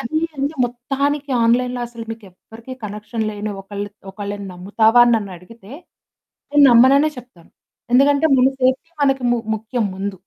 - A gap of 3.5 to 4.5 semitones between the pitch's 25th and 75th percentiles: Yes, average, 4.2 semitones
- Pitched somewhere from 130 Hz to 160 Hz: No, high, 235 Hz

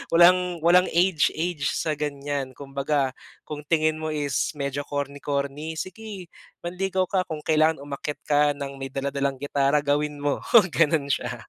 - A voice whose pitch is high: No, medium, 150 Hz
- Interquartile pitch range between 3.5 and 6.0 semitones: No, average, 2.8 semitones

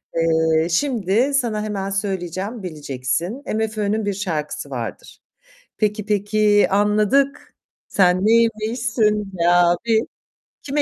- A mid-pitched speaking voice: No, high, 205 Hz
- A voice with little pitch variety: No, average, 4.0 semitones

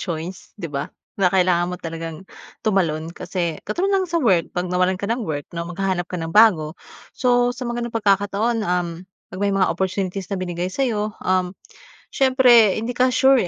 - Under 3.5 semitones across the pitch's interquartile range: No, average, 4.6 semitones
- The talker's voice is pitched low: No, high, 190 Hz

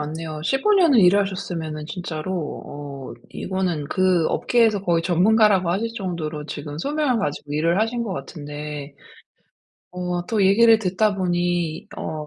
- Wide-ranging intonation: No, average, 4.7 semitones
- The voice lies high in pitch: No, medium, 180 Hz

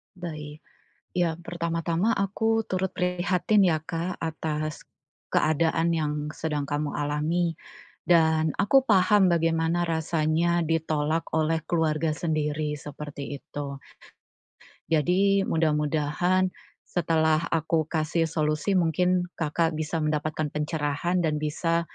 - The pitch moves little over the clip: Yes, narrow, 2.2 semitones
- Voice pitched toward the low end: No, medium, 160 Hz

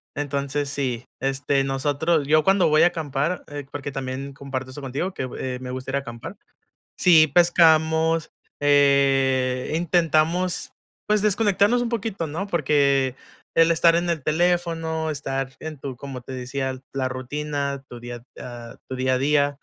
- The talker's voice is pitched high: No, medium, 145 Hz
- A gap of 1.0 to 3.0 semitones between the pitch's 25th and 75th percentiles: No, average, 3.6 semitones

